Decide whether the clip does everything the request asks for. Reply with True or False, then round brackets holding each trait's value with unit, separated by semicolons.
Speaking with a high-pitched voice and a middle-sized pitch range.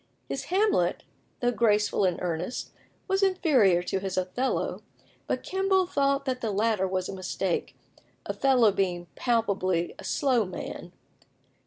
False (220 Hz; 6.8 semitones)